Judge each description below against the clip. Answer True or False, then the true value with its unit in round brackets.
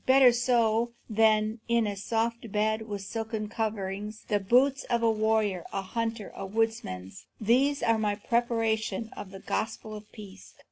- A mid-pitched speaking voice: False (220 Hz)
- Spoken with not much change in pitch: True (1.9 semitones)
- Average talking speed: True (155 wpm)